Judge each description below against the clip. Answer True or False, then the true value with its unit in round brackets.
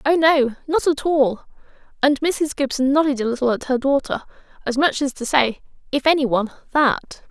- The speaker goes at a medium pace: True (180 wpm)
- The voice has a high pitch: True (275 Hz)